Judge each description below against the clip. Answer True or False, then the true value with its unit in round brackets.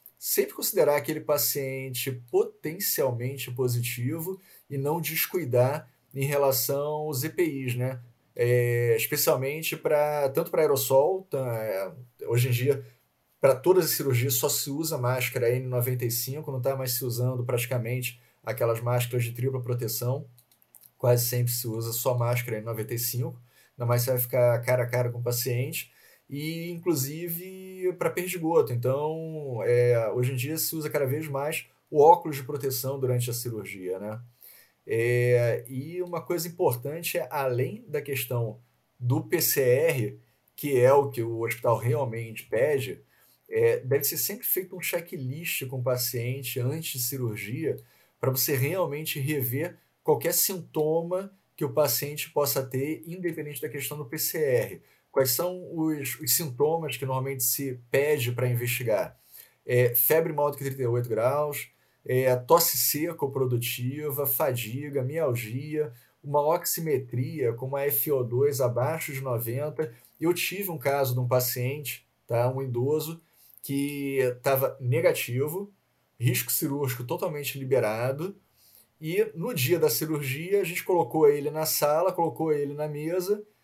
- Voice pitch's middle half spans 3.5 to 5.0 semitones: True (4.1 semitones)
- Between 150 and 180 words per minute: False (140 wpm)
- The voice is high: False (135 Hz)